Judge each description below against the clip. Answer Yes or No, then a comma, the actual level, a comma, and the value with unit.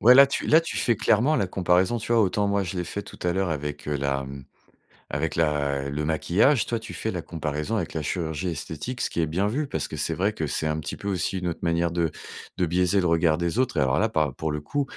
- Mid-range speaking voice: No, very low, 85 Hz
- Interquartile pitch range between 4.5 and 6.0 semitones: Yes, average, 5.1 semitones